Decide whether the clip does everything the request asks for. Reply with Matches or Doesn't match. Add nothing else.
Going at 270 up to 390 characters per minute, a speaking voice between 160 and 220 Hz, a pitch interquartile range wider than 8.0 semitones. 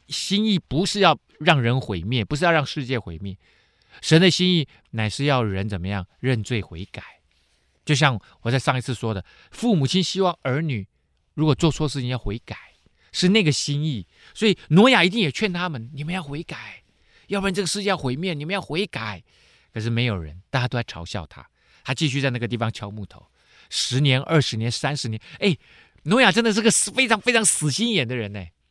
Doesn't match